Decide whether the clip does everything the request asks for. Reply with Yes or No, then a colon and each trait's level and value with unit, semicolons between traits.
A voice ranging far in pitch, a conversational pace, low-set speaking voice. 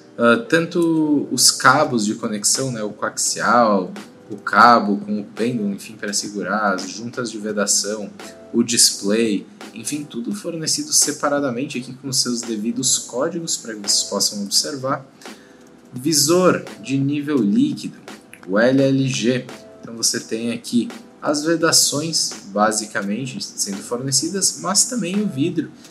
Yes: wide, 6.2 semitones; average, 130 wpm; low, 130 Hz